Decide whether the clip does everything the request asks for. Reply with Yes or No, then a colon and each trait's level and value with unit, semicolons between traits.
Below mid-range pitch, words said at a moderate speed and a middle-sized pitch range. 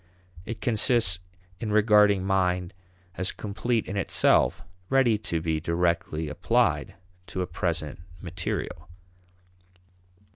No: very low, 95 Hz; slow, 105 wpm; average, 3.9 semitones